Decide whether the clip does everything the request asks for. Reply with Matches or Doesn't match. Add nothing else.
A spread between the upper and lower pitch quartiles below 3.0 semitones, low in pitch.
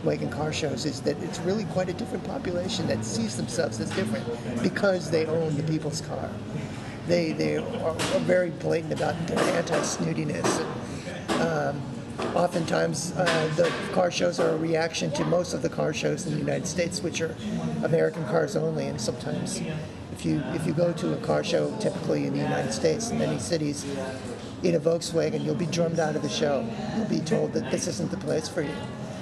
Doesn't match